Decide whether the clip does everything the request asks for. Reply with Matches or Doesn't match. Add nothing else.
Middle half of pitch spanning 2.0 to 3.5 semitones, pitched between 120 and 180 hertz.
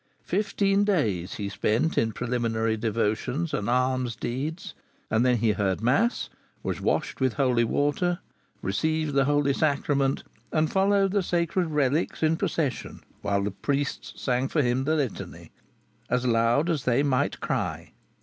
Doesn't match